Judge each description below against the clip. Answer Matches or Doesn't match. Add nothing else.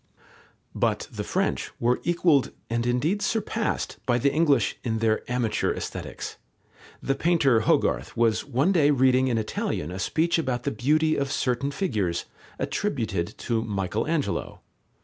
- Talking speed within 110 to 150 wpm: Matches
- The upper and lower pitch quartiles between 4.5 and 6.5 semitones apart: Matches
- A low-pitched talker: Matches